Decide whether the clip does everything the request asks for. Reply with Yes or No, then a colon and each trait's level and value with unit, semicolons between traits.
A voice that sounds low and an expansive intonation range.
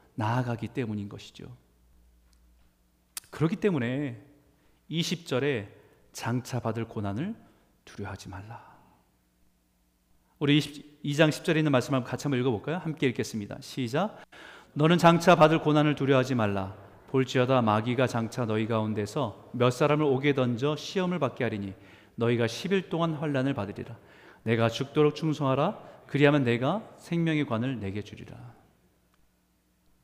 Yes: low, 125 Hz; wide, 6.2 semitones